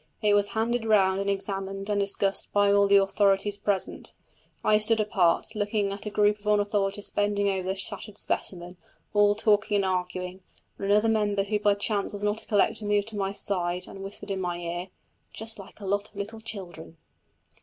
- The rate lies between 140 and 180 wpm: No, average, 195 wpm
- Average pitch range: No, narrow, 1.2 semitones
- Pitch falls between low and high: No, high, 200 Hz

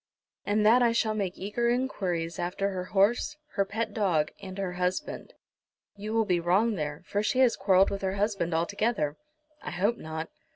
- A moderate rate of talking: Yes, average, 180 wpm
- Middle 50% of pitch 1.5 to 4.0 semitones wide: Yes, average, 3.3 semitones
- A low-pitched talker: No, high, 195 Hz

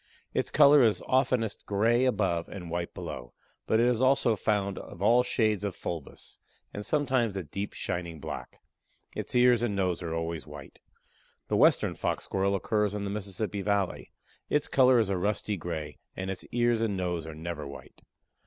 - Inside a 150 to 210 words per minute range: Yes, average, 180 wpm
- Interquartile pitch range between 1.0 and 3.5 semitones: No, average, 5.0 semitones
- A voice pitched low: Yes, low, 100 Hz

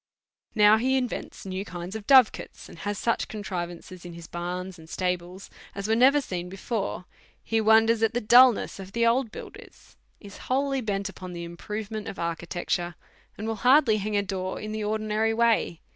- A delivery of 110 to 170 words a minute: No, average, 190 wpm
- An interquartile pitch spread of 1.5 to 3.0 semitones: No, average, 3.6 semitones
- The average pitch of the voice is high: Yes, high, 210 Hz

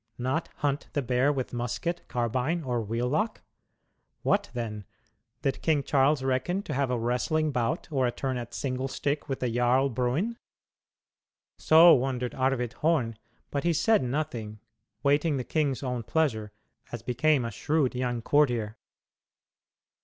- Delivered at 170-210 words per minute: No, average, 150 wpm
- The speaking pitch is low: Yes, low, 130 Hz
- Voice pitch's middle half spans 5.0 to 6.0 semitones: No, average, 3.6 semitones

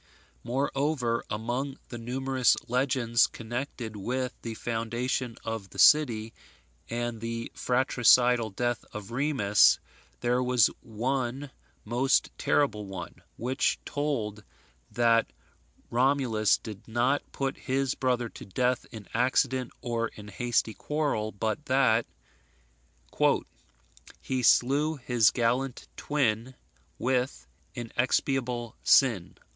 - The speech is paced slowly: Yes, slow, 105 wpm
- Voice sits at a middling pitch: No, low, 120 Hz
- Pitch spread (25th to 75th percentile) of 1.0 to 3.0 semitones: Yes, narrow, 2.5 semitones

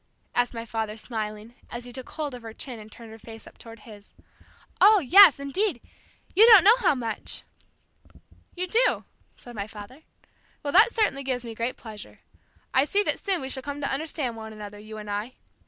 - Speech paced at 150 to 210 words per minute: Yes, average, 200 wpm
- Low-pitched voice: No, high, 245 Hz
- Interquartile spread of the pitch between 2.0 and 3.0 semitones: No, average, 5.3 semitones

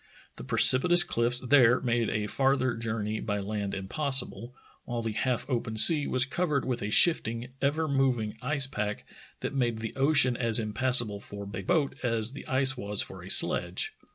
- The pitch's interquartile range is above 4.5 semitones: No, average, 3.6 semitones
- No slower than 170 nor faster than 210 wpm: Yes, average, 180 wpm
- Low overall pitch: Yes, low, 120 Hz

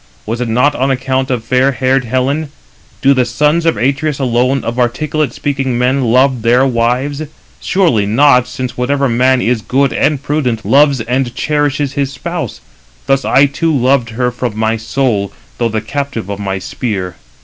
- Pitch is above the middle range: No, low, 130 Hz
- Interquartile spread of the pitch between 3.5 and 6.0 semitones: No, average, 2.8 semitones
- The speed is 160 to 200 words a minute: Yes, average, 170 wpm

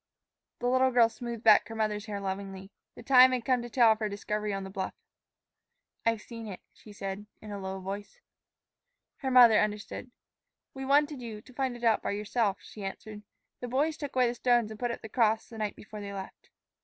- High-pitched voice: Yes, high, 220 Hz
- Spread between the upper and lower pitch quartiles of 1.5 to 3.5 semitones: Yes, average, 3.1 semitones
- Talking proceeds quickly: Yes, fast, 215 wpm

